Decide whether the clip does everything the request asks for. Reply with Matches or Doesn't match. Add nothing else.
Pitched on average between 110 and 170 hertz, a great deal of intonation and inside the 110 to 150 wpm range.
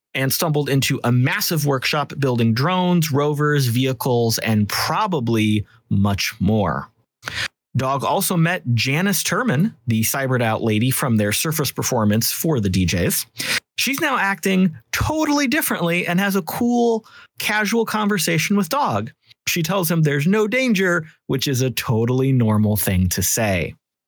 Matches